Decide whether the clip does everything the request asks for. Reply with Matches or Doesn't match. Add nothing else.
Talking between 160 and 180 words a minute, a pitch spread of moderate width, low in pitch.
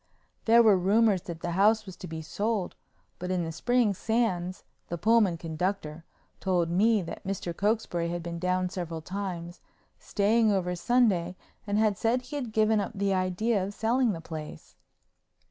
Doesn't match